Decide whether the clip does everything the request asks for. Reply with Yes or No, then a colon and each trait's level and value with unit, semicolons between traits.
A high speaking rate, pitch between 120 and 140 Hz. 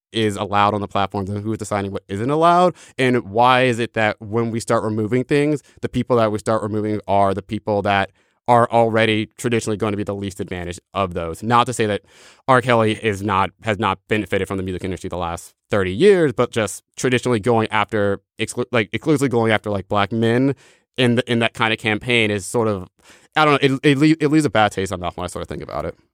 No: fast, 240 wpm; low, 110 Hz